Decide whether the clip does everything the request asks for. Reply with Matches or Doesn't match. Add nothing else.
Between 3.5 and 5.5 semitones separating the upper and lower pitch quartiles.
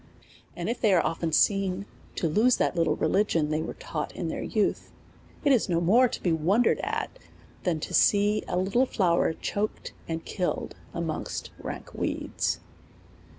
Matches